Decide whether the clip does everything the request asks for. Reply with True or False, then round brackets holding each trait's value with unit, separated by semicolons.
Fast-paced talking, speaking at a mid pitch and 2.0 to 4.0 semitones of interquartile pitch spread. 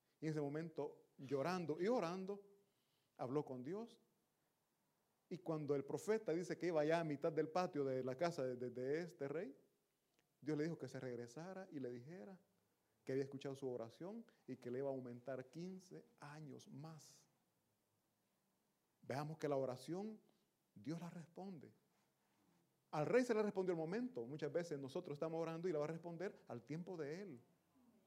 False (175 wpm; 155 Hz; 4.8 semitones)